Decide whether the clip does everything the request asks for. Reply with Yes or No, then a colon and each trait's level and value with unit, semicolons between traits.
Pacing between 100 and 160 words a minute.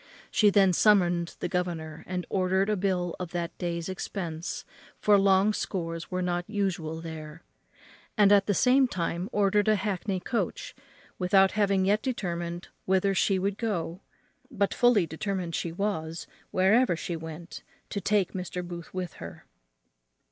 Yes: average, 150 wpm